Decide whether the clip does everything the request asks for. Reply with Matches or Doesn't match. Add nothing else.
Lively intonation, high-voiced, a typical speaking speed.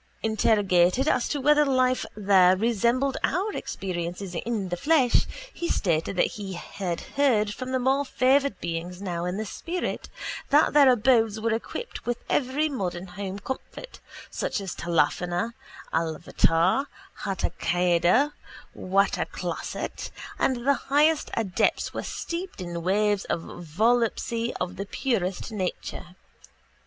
Doesn't match